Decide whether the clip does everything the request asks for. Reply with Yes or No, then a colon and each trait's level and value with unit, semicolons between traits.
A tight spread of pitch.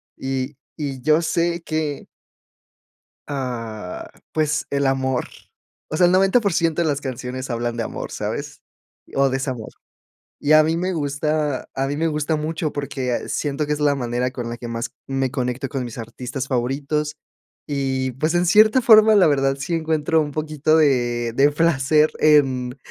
No: average, 3.3 semitones